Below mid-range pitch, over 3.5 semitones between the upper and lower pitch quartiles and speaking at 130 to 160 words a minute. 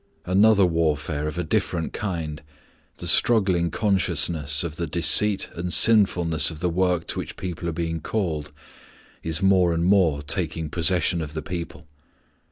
No: very low, 85 Hz; average, 2.8 semitones; average, 155 wpm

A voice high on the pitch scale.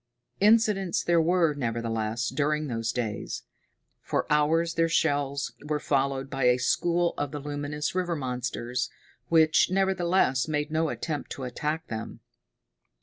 No: medium, 150 Hz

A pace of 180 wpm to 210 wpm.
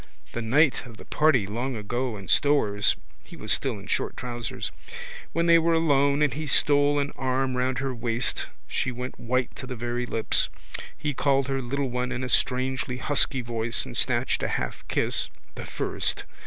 Yes: average, 185 wpm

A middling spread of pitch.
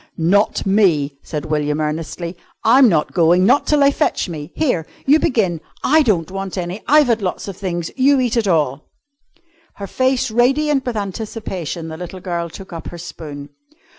No: wide, 6.7 semitones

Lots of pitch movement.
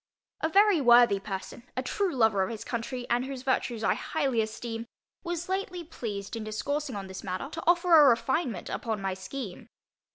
Yes: wide, 6.2 semitones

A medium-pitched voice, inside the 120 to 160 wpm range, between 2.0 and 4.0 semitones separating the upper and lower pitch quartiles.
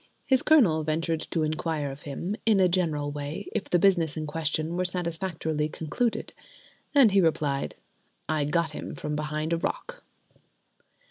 Yes: medium, 160 Hz; average, 155 wpm; average, 3.2 semitones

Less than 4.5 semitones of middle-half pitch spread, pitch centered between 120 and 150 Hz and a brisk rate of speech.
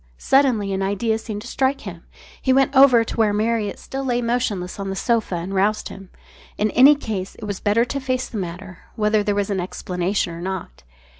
No: average, 3.8 semitones; high, 210 Hz; fast, 210 wpm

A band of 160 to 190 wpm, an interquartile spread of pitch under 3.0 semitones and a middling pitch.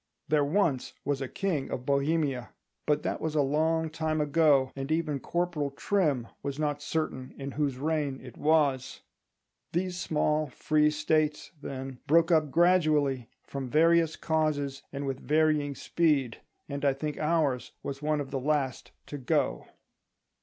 No: average, 150 wpm; narrow, 2.5 semitones; medium, 150 Hz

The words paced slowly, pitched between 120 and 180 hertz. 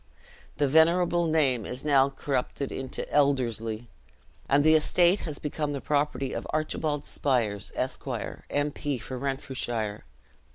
Yes: slow, 130 wpm; medium, 140 Hz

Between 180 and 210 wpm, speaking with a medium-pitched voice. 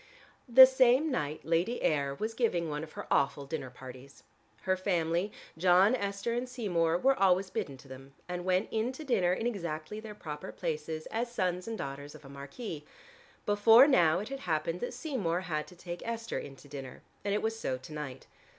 Yes: average, 195 wpm; medium, 180 Hz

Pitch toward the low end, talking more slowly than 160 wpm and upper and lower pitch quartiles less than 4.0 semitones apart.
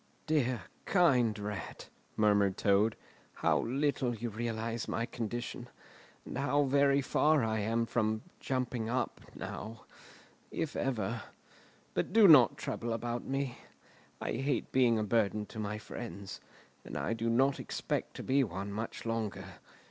Yes: low, 115 Hz; average, 140 wpm; average, 3.3 semitones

